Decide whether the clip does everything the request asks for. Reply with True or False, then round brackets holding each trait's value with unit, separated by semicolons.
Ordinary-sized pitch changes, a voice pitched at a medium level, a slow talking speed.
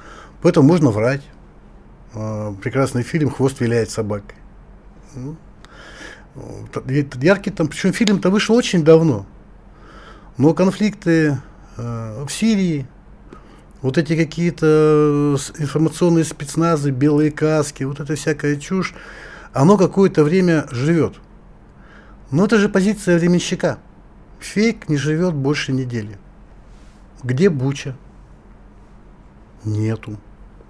True (5.0 semitones; 150 Hz; 95 wpm)